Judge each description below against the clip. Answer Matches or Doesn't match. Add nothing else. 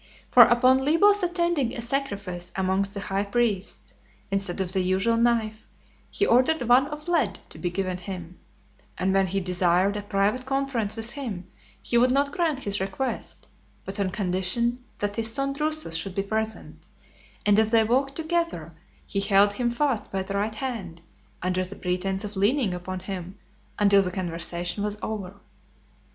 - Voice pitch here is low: Doesn't match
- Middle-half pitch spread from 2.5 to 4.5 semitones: Doesn't match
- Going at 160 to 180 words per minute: Matches